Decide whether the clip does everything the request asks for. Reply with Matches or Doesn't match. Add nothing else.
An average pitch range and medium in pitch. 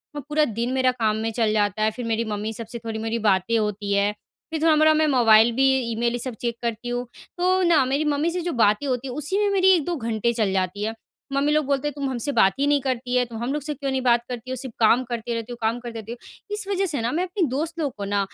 Doesn't match